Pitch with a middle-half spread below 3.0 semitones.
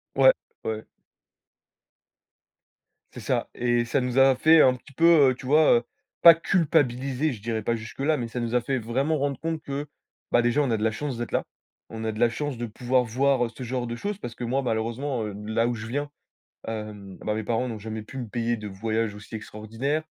No: average, 3.6 semitones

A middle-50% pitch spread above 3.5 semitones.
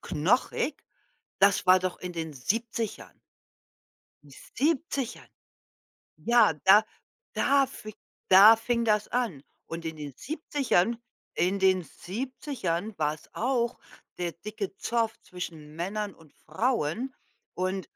Yes: wide, 5.6 semitones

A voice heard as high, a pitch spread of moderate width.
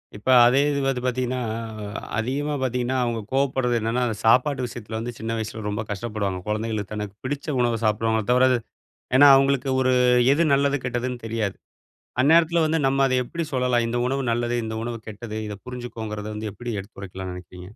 No: low, 120 Hz; average, 3.1 semitones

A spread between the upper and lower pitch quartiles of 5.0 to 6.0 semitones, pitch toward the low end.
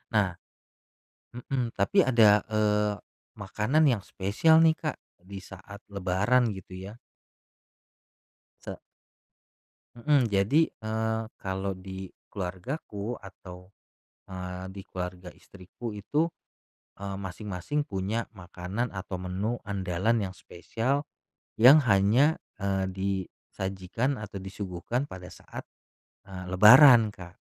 No: average, 3.8 semitones; low, 100 Hz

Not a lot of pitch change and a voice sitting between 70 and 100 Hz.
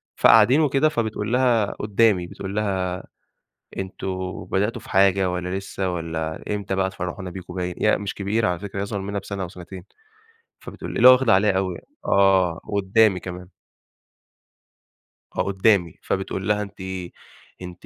Yes: narrow, 2.2 semitones; very low, 95 Hz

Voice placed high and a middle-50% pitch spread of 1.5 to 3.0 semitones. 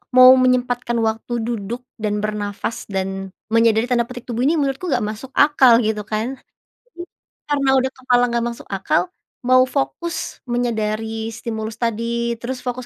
Yes: high, 235 Hz; narrow, 2.4 semitones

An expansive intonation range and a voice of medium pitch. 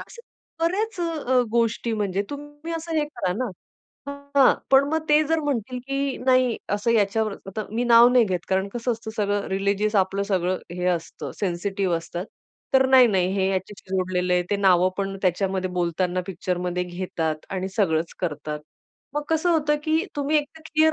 No: wide, 7.1 semitones; high, 205 Hz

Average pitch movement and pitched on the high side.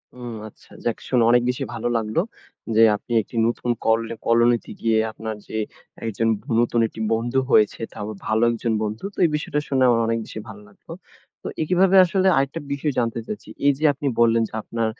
No: average, 3.1 semitones; low, 115 Hz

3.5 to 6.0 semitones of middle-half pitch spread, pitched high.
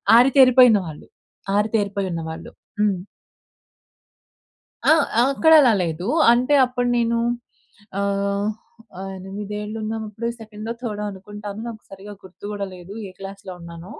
No: average, 2.8 semitones; high, 210 Hz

